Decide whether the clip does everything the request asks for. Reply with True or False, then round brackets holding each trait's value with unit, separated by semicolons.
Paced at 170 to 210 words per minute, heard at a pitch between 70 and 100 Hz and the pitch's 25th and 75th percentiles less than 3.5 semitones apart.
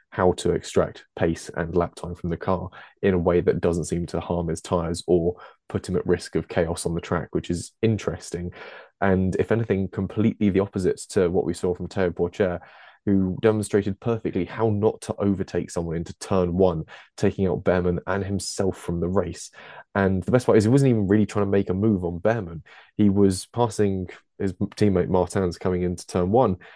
True (205 wpm; 95 Hz; 2.5 semitones)